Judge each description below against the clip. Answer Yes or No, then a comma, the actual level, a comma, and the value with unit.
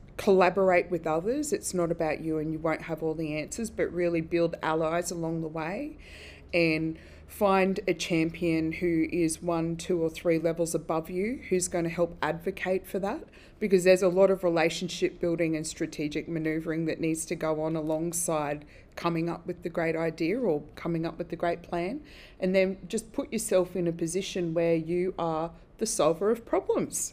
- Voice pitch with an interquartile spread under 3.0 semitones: Yes, narrow, 2.5 semitones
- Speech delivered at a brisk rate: No, average, 190 wpm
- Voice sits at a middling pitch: Yes, medium, 170 Hz